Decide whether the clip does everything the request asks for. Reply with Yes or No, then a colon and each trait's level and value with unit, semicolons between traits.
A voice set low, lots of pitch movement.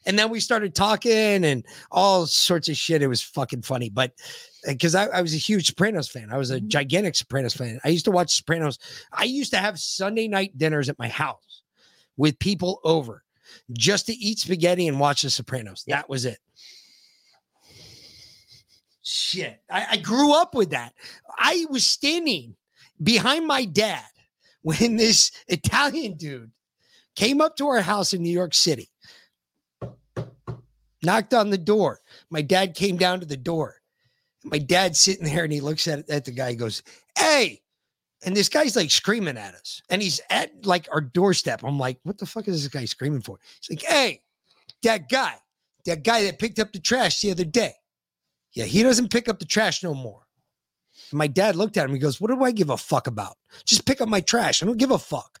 No: medium, 180 Hz; wide, 7.3 semitones